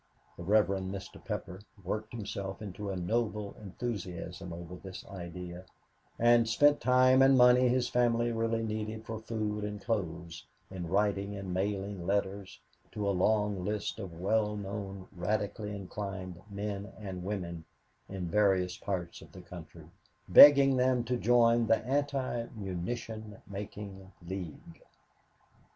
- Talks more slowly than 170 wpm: Yes, slow, 135 wpm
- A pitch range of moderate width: Yes, average, 3.1 semitones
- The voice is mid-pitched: No, low, 105 Hz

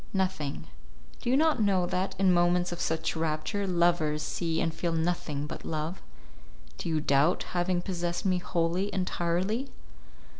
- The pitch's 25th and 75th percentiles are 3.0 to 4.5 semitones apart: No, narrow, 2.5 semitones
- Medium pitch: Yes, medium, 175 Hz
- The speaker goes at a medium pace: Yes, average, 150 wpm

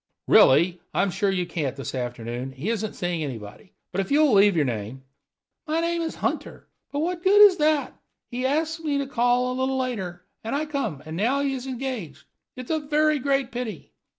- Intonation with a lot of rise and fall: Yes, wide, 8.8 semitones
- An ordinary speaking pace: No, fast, 210 wpm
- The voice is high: Yes, high, 245 Hz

